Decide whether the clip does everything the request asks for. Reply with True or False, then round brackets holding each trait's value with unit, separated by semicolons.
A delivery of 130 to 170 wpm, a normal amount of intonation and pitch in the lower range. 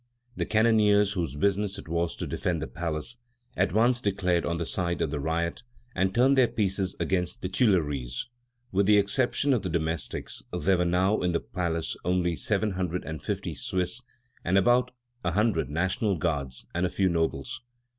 False (180 wpm; 3.7 semitones; 90 Hz)